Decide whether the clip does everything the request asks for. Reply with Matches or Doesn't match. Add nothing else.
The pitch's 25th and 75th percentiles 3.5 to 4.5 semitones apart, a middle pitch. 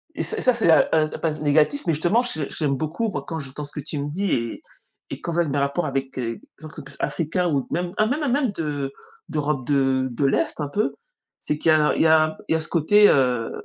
Matches